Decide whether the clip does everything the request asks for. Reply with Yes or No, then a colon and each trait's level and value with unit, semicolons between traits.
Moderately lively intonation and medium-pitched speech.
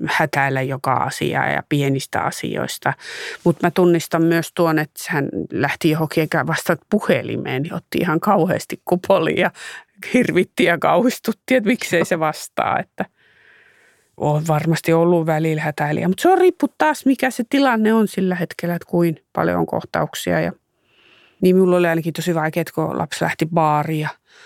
Yes: average, 3.6 semitones; medium, 170 Hz